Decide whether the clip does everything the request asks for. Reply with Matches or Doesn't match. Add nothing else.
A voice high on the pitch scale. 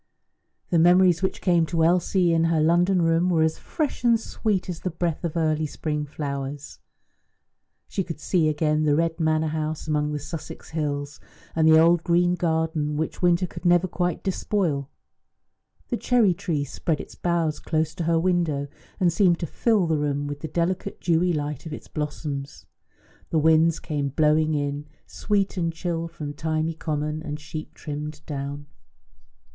Doesn't match